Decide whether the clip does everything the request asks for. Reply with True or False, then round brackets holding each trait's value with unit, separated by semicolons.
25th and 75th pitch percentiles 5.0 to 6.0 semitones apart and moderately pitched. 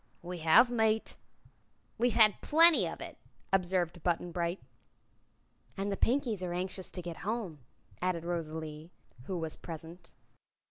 False (3.9 semitones; 180 Hz)